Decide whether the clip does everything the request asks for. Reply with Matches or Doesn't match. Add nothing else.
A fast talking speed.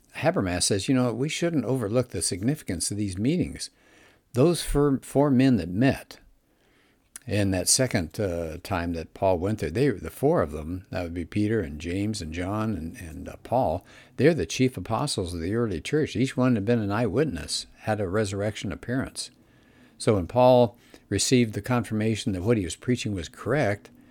Doesn't match